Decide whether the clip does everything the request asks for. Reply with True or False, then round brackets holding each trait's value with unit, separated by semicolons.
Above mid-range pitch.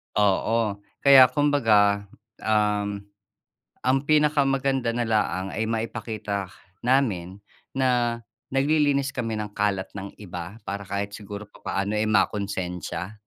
False (105 Hz)